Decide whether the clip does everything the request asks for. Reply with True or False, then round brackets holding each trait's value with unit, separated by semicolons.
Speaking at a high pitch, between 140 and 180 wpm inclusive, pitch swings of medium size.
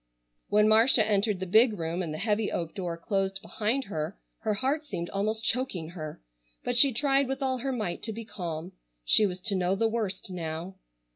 False (205 Hz; 200 wpm; 4.2 semitones)